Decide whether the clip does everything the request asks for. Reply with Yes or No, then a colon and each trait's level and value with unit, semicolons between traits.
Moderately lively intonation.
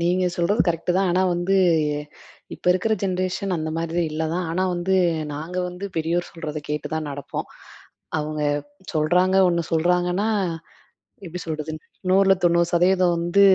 No: narrow, 2.3 semitones